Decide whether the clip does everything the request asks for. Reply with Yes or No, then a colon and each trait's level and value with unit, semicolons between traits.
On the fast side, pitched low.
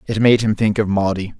Yes: fast, 260 wpm; low, 105 Hz